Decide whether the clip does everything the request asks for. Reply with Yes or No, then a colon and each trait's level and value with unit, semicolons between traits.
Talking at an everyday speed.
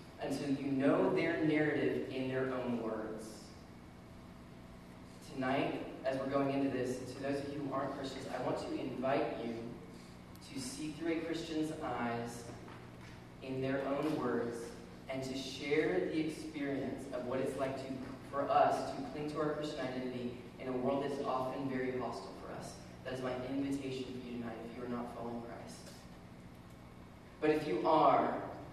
Yes: average, 170 wpm